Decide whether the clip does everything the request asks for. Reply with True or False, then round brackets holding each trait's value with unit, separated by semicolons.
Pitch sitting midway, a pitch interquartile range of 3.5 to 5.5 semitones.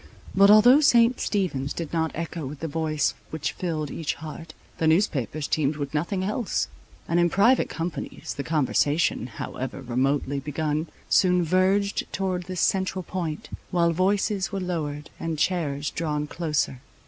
True (165 Hz; 3.9 semitones)